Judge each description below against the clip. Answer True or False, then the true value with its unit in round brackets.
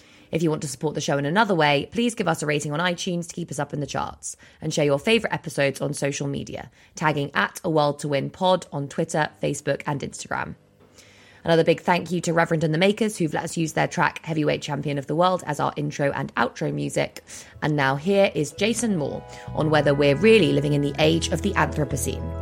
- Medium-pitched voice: True (155 Hz)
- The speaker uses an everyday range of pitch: True (3.4 semitones)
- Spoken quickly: True (235 wpm)